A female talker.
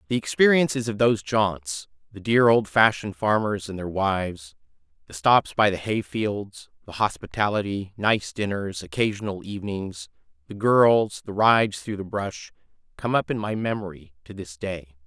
No: male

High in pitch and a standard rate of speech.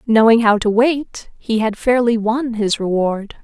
Yes: high, 225 Hz; average, 175 wpm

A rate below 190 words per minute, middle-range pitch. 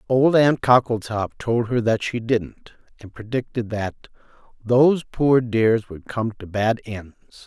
No: average, 155 wpm; low, 115 Hz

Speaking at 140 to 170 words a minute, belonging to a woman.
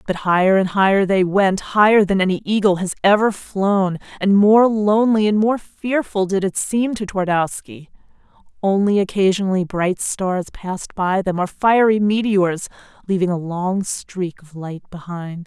Yes: average, 150 wpm; female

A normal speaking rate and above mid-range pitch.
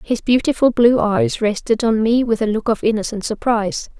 Yes: average, 195 wpm; high, 220 Hz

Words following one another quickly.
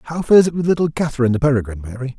Yes: fast, 245 wpm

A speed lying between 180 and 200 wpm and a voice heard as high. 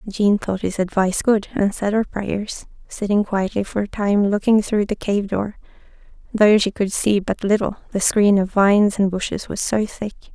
Yes: average, 195 wpm; high, 205 Hz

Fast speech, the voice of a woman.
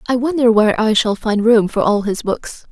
Yes: fast, 245 wpm; female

